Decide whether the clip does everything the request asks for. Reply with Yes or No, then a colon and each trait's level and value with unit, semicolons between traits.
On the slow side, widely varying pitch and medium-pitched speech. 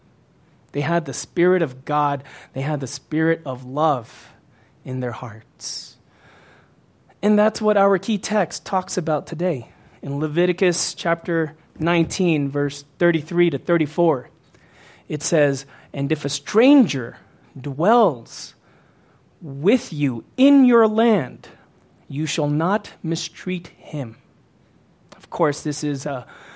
No: slow, 120 wpm; average, 4.2 semitones; medium, 155 Hz